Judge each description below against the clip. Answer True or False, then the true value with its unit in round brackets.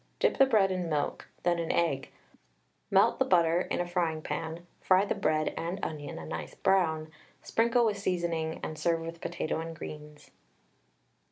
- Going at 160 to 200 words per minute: True (170 wpm)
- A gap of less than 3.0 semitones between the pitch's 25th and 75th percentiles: True (2.6 semitones)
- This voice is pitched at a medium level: True (165 Hz)